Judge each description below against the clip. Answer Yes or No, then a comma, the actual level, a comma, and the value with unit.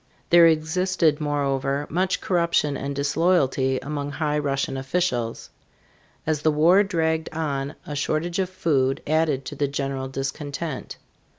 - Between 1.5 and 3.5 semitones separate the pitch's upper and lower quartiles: Yes, average, 3.1 semitones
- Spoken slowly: Yes, slow, 130 wpm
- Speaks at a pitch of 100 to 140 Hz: No, medium, 150 Hz